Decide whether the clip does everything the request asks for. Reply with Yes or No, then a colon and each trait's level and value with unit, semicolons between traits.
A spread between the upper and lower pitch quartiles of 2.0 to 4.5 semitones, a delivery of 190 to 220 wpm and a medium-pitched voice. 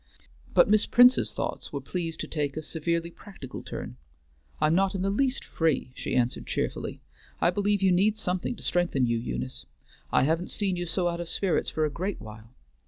No: wide, 5.4 semitones; average, 195 wpm; medium, 170 Hz